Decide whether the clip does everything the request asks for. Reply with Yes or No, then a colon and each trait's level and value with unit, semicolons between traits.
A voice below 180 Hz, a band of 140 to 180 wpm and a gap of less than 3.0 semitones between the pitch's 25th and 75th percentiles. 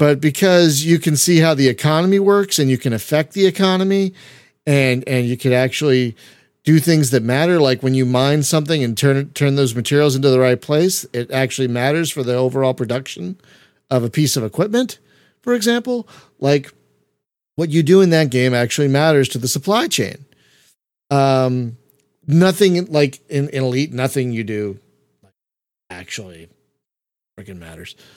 No: medium, 140 Hz; average, 165 wpm; average, 4.3 semitones